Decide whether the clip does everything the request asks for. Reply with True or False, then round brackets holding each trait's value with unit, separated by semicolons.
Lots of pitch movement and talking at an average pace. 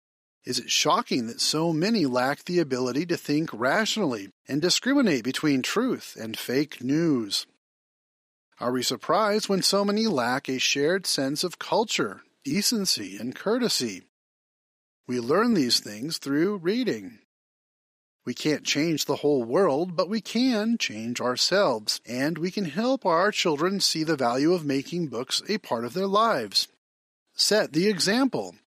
True (7.1 semitones; 150 wpm)